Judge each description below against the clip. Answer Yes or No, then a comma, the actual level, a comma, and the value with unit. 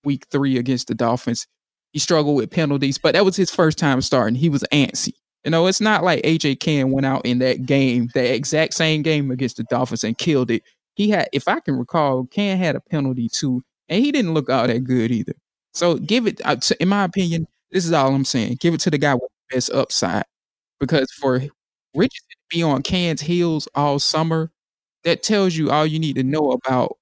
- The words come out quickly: Yes, fast, 220 wpm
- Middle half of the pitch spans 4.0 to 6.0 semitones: Yes, average, 4.3 semitones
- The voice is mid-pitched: Yes, medium, 145 Hz